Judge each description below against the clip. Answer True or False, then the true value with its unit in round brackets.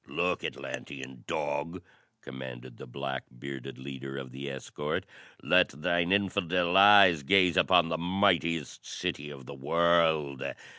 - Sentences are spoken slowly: True (130 wpm)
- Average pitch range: True (4.4 semitones)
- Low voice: True (75 Hz)